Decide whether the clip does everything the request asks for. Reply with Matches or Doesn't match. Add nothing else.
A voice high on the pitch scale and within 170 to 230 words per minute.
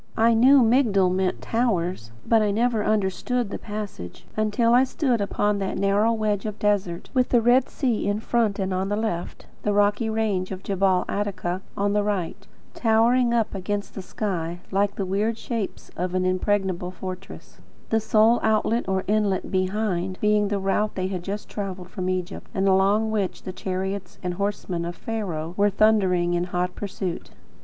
Matches